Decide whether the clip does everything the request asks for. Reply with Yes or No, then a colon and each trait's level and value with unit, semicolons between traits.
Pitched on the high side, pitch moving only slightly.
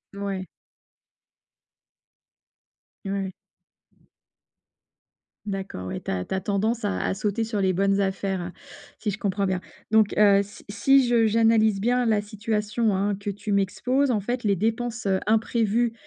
Yes: high, 205 Hz; narrow, 2.3 semitones